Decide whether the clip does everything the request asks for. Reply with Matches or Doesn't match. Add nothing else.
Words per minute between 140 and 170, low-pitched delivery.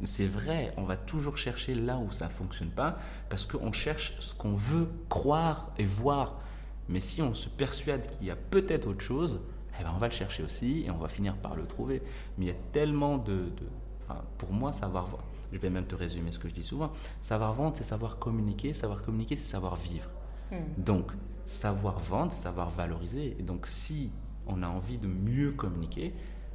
Doesn't match